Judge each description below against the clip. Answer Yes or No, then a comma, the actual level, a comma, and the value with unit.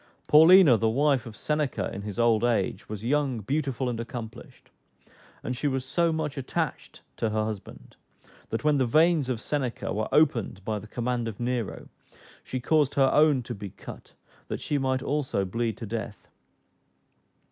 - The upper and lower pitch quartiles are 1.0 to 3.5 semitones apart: No, average, 4.4 semitones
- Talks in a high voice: No, low, 125 Hz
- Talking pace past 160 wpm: Yes, average, 170 wpm